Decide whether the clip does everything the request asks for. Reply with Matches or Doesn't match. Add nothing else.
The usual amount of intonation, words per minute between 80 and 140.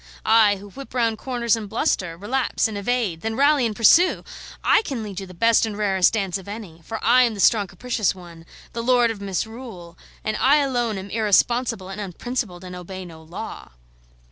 Doesn't match